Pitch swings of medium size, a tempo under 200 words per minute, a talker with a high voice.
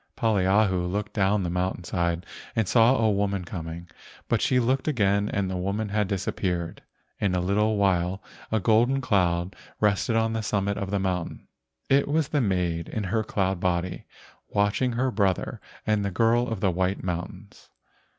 No: average, 3.2 semitones; average, 170 wpm; low, 100 Hz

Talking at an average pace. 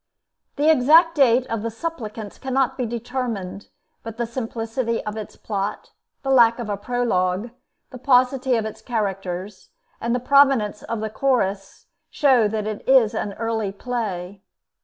Yes: average, 155 wpm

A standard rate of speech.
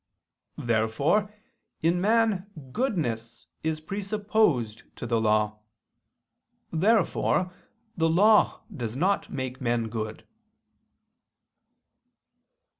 No: slow, 80 wpm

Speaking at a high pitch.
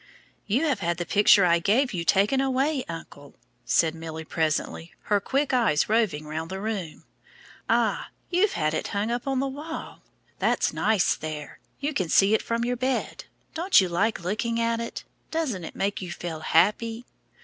Yes: high, 205 Hz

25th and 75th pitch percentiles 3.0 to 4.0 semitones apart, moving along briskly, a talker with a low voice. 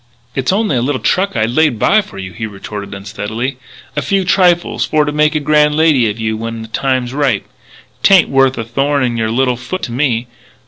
No: average, 4.9 semitones; fast, 220 wpm; low, 130 Hz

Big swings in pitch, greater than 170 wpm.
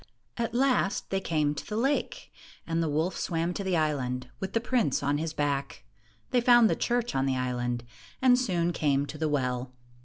Yes: wide, 8.0 semitones; average, 195 wpm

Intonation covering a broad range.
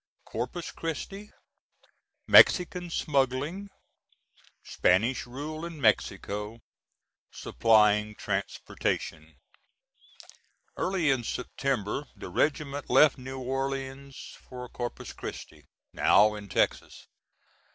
Yes: wide, 5.8 semitones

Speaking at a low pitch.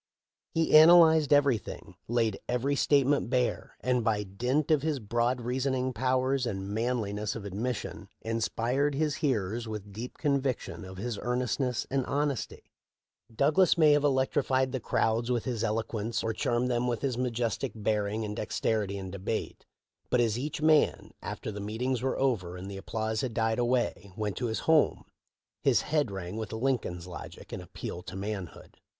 Yes: low, 120 Hz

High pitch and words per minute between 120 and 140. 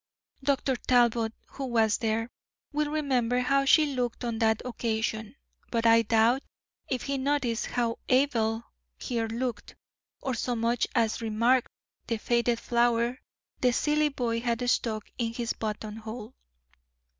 Yes: high, 235 Hz; slow, 135 wpm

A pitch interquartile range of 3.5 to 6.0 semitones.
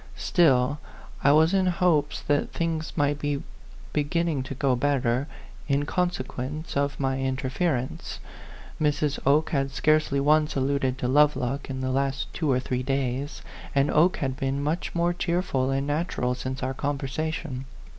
No: average, 2.7 semitones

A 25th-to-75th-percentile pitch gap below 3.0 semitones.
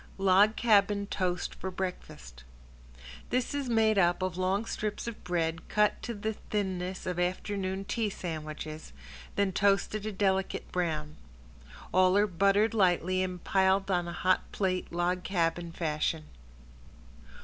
Yes: narrow, 2.5 semitones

